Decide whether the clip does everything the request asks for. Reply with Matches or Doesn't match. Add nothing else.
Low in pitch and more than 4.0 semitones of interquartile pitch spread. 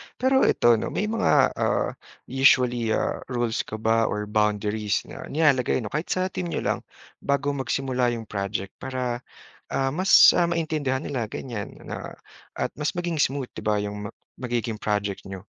Matches